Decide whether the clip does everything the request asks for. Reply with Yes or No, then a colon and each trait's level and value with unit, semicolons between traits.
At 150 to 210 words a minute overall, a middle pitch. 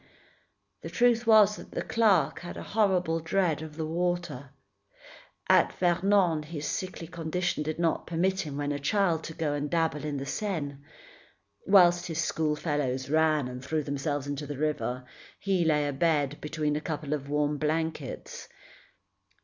Yes: average, 155 wpm; medium, 155 Hz